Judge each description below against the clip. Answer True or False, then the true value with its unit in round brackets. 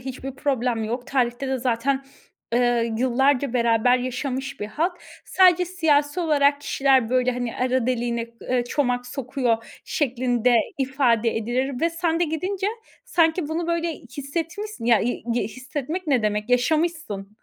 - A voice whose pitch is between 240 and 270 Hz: True (260 Hz)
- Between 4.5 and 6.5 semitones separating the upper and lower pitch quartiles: False (4.0 semitones)